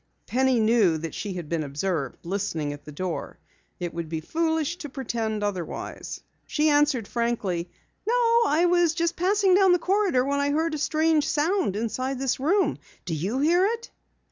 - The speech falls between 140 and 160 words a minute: No, average, 170 wpm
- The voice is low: No, very high, 265 Hz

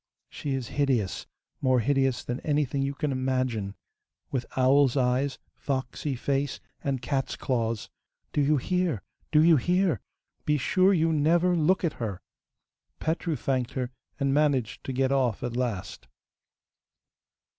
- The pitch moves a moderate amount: Yes, average, 3.1 semitones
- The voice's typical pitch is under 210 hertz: Yes, low, 135 Hz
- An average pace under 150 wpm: Yes, average, 140 wpm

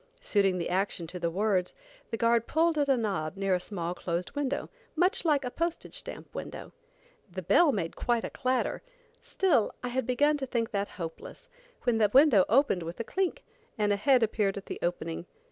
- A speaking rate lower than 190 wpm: No, average, 195 wpm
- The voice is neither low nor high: No, high, 225 Hz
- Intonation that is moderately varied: No, wide, 6.9 semitones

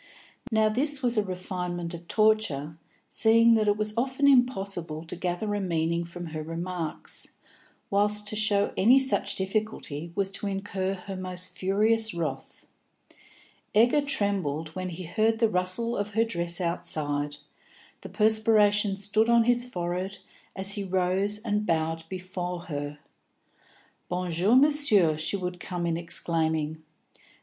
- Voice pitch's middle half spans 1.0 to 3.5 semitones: No, average, 4.0 semitones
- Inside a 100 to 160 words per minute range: Yes, average, 140 wpm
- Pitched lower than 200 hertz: Yes, high, 190 Hz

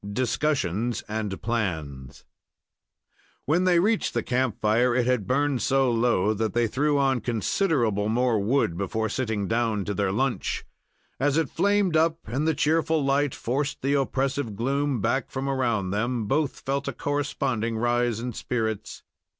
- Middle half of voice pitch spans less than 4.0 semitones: No, average, 4.3 semitones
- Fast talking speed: No, average, 155 wpm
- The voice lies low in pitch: Yes, low, 125 Hz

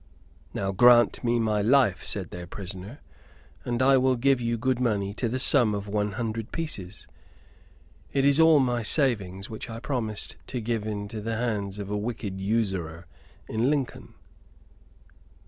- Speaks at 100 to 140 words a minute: No, average, 160 wpm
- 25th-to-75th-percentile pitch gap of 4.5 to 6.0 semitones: No, average, 3.5 semitones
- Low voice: Yes, low, 115 Hz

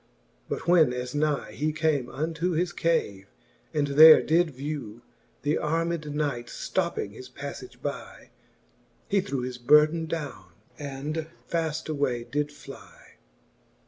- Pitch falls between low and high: Yes, medium, 150 Hz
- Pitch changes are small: No, average, 3.5 semitones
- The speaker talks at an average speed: No, slow, 130 wpm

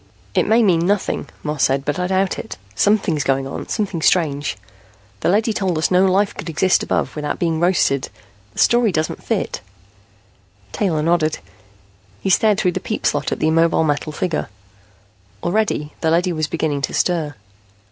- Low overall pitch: No, medium, 170 Hz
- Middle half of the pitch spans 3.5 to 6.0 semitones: Yes, average, 3.8 semitones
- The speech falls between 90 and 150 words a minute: No, average, 170 wpm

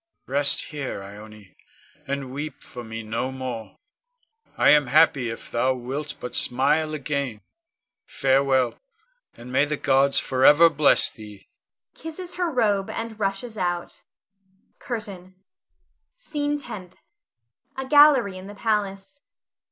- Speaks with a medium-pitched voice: Yes, medium, 150 Hz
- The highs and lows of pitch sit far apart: Yes, wide, 7.9 semitones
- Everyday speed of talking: No, slow, 120 wpm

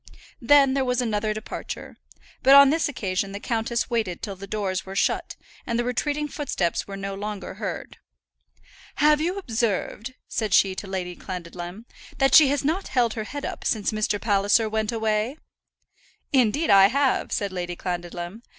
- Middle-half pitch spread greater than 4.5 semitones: Yes, average, 5.1 semitones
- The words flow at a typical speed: Yes, average, 170 wpm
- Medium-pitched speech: No, high, 215 Hz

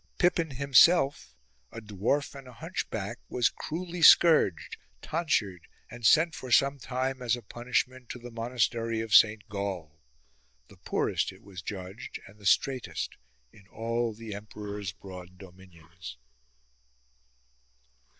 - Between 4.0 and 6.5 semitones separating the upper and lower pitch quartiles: Yes, average, 4.8 semitones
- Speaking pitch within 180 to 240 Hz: No, low, 115 Hz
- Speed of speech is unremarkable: No, slow, 130 wpm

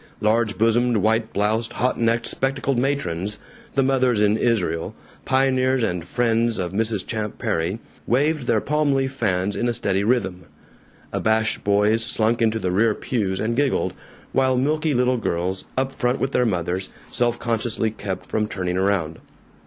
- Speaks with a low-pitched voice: Yes, low, 115 Hz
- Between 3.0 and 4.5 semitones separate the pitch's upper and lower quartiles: Yes, average, 3.9 semitones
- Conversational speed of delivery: Yes, average, 160 wpm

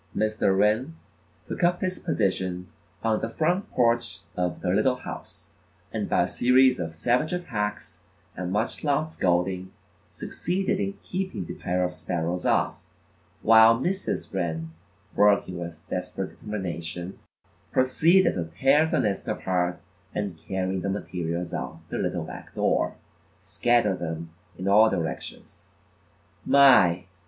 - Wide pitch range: Yes, wide, 6.3 semitones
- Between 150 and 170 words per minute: No, slow, 135 wpm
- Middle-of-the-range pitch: No, low, 100 Hz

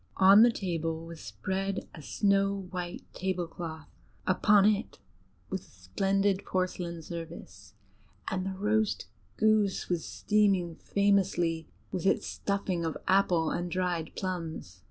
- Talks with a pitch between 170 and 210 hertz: Yes, medium, 185 Hz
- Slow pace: Yes, slow, 125 wpm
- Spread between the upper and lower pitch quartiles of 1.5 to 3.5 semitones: Yes, average, 2.9 semitones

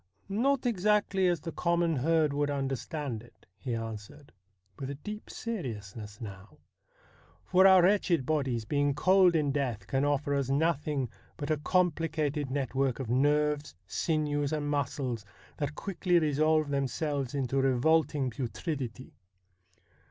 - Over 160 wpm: No, average, 140 wpm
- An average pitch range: Yes, average, 3.6 semitones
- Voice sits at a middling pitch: Yes, medium, 145 Hz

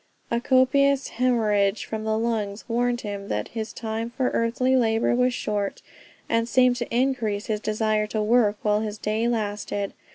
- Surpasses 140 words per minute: Yes, average, 165 wpm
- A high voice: Yes, high, 225 Hz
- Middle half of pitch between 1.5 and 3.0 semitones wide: Yes, narrow, 2.4 semitones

